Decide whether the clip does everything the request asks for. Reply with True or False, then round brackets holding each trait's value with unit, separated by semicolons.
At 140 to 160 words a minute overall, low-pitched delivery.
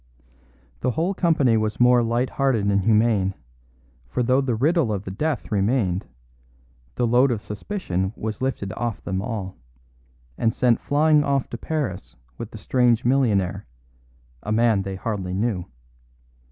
True (145 wpm; 115 Hz)